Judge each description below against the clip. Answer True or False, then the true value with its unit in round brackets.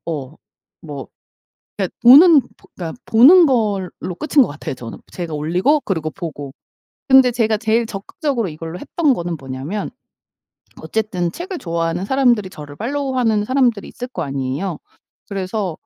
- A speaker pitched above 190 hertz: True (200 Hz)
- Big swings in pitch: True (7.3 semitones)